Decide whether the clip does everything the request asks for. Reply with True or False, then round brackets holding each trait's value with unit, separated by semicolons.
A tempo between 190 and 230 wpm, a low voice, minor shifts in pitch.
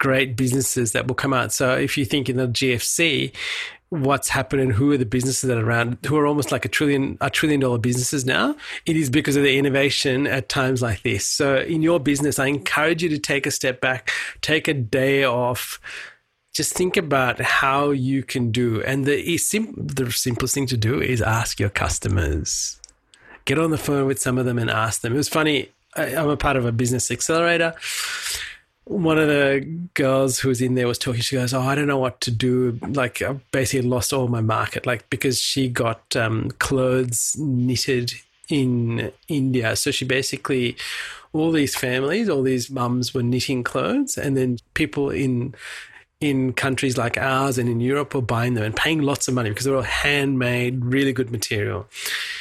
True (200 wpm; 130 Hz; 2.3 semitones)